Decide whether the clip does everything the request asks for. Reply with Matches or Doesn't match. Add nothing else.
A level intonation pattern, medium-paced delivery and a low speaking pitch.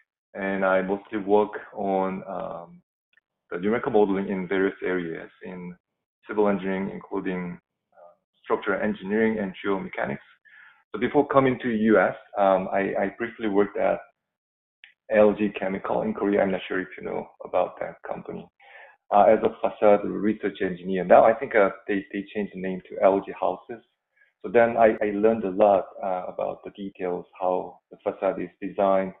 Matches